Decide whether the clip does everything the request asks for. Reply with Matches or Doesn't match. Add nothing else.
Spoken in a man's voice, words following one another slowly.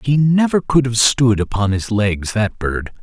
Doesn't match